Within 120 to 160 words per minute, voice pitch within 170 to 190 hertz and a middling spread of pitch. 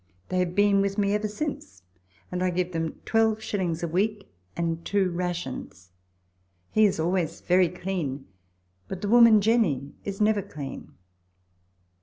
Yes: average, 145 wpm; medium, 185 Hz; average, 3.6 semitones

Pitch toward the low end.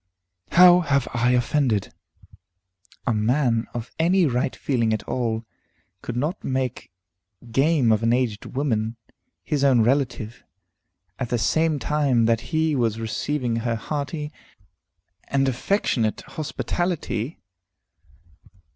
Yes: low, 125 Hz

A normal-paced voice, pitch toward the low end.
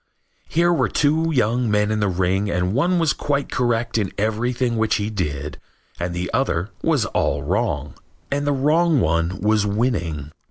Yes: average, 170 wpm; low, 110 Hz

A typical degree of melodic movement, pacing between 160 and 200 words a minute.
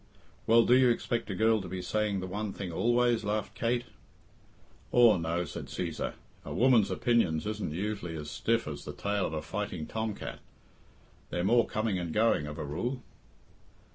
Yes: average, 4.8 semitones; average, 180 wpm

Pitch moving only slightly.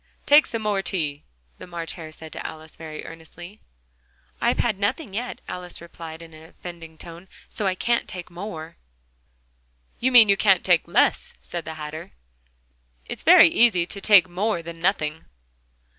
No: average, 3.7 semitones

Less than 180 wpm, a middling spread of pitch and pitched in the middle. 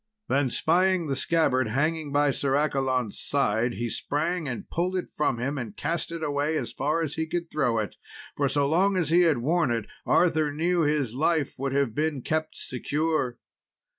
No: average, 190 wpm; average, 3.7 semitones; medium, 145 Hz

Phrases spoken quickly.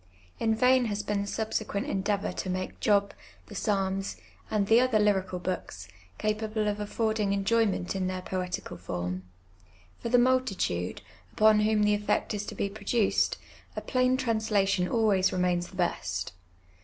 No: average, 155 wpm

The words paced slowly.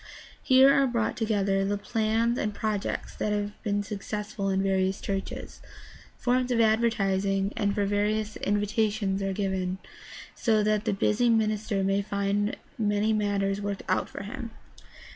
No: average, 150 wpm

